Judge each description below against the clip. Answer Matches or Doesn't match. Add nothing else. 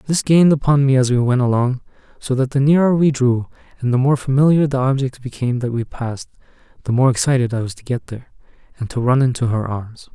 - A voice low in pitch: Matches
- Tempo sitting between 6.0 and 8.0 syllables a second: Matches